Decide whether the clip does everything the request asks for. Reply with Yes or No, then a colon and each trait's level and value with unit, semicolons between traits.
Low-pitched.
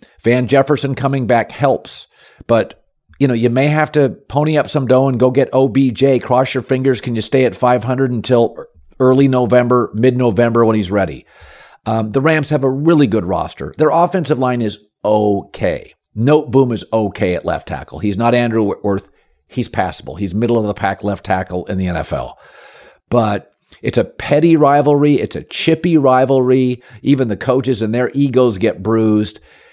Yes: low, 125 Hz